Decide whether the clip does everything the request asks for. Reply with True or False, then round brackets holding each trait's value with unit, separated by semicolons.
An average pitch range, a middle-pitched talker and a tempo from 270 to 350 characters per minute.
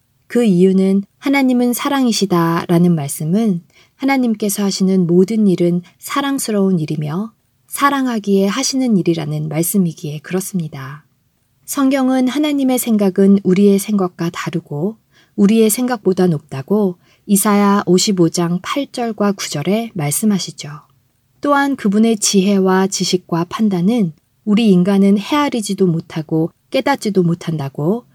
False (4.7 semitones; 195 Hz; 290 characters per minute)